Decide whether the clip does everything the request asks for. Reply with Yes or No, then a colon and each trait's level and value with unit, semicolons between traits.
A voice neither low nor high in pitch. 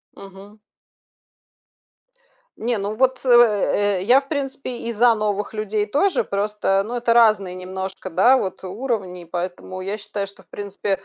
No: high, 205 Hz